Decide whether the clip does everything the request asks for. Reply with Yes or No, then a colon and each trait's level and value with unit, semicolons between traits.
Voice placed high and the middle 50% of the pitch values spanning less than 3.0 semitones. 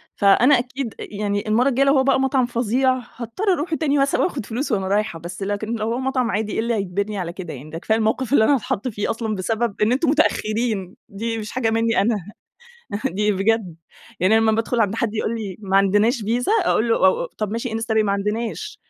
No: high, 225 Hz; average, 3.3 semitones